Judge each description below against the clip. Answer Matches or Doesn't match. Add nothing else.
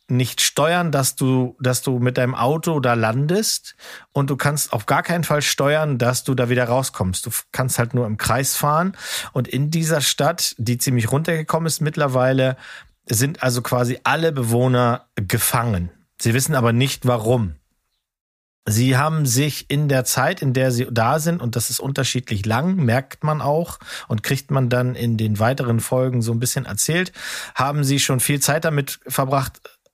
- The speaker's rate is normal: Matches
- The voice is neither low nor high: Doesn't match